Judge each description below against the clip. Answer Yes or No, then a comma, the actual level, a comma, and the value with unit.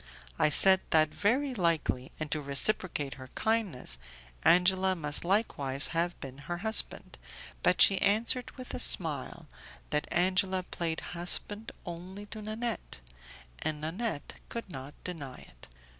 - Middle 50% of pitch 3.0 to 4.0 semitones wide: No, wide, 5.6 semitones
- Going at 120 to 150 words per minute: Yes, slow, 135 wpm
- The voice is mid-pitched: Yes, medium, 175 Hz